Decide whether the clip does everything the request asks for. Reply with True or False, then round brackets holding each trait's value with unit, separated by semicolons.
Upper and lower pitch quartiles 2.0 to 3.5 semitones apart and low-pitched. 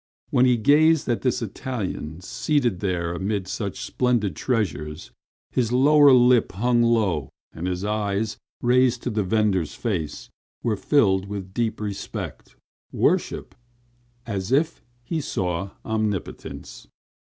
False (4.6 semitones; 110 Hz)